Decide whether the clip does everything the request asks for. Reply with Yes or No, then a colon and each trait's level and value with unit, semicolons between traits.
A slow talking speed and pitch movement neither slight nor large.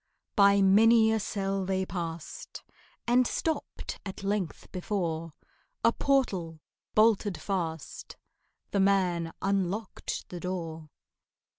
Yes: slow, 105 wpm; average, 3.4 semitones